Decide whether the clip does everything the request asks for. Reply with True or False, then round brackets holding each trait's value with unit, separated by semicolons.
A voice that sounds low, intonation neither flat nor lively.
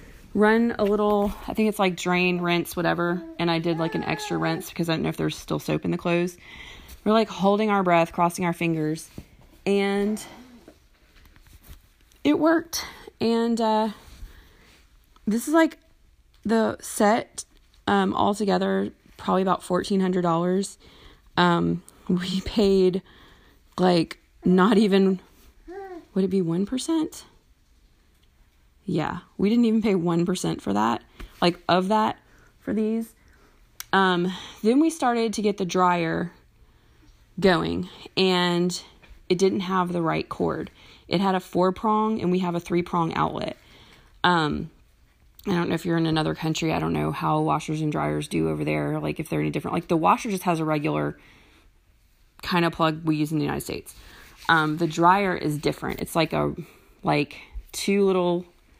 False (180 Hz; 4.5 semitones)